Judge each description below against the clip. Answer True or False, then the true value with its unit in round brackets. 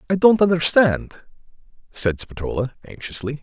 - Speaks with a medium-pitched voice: True (150 Hz)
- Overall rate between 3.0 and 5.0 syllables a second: True (4.8 syllables/s)